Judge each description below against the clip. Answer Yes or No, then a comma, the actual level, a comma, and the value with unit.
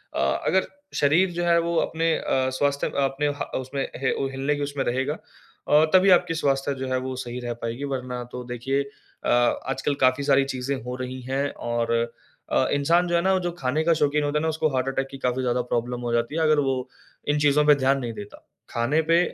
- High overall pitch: No, medium, 140 Hz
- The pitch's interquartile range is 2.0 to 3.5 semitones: Yes, average, 2.9 semitones